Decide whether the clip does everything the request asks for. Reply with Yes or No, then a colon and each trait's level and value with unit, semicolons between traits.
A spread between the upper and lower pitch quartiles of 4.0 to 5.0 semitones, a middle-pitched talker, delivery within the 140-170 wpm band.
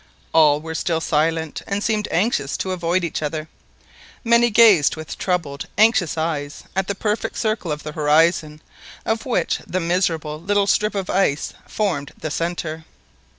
Yes: average, 4.5 semitones; medium, 170 Hz; average, 155 wpm